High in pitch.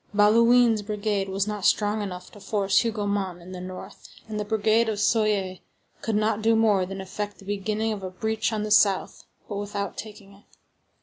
Yes: high, 205 Hz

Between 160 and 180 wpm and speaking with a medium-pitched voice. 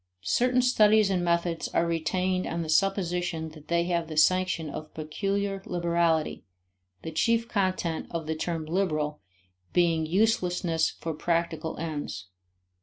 No: slow, 135 wpm; medium, 170 Hz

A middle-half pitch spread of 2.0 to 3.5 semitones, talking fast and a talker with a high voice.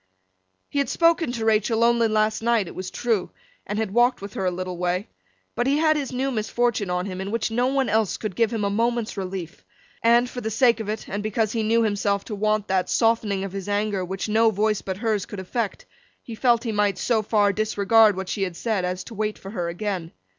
Yes: average, 3.0 semitones; fast, 235 wpm; high, 215 Hz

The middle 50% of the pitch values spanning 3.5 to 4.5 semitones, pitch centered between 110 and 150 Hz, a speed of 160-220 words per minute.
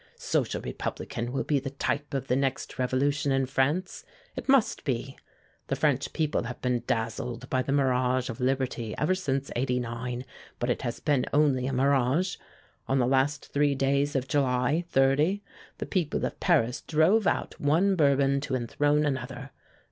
No: narrow, 2.5 semitones; low, 135 Hz; average, 165 wpm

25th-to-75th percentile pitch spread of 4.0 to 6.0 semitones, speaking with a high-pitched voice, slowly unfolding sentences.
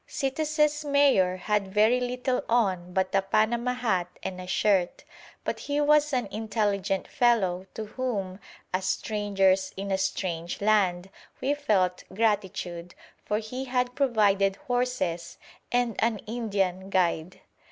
Yes: average, 4.8 semitones; high, 210 Hz; slow, 130 wpm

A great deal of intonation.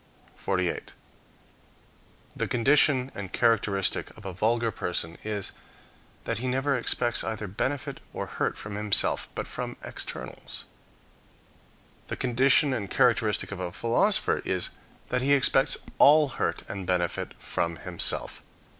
No: average, 4.9 semitones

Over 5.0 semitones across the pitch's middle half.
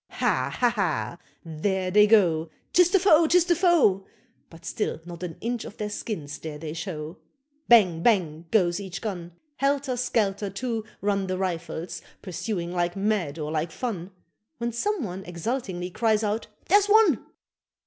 Yes: wide, 5.6 semitones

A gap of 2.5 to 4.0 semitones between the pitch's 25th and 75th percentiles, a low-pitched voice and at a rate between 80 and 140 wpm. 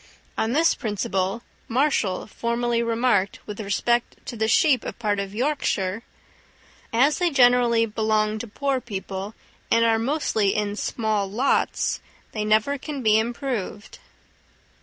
No: average, 2.9 semitones; high, 225 Hz; slow, 135 wpm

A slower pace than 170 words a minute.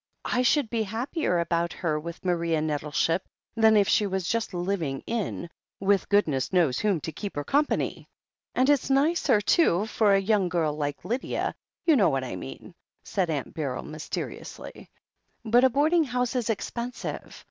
No: average, 175 wpm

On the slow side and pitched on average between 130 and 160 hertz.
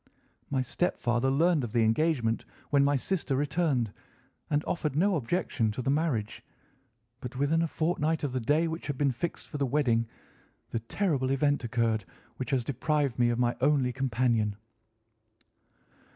No: average, 160 wpm; low, 135 Hz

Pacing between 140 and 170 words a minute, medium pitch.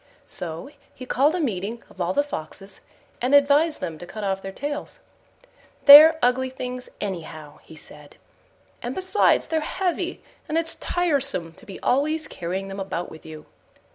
No: average, 165 wpm; very high, 250 Hz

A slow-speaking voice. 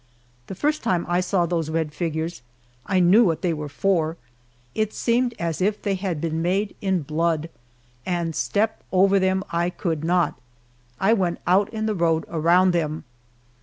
No: average, 170 wpm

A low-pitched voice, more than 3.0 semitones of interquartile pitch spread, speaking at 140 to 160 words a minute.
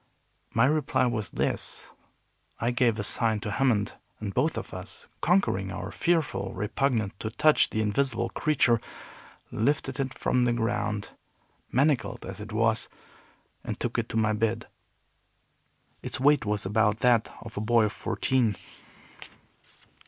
Yes: low, 115 Hz; average, 3.6 semitones; average, 145 wpm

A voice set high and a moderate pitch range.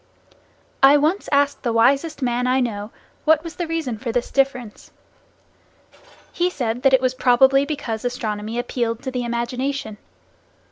Yes: very high, 255 Hz; average, 3.0 semitones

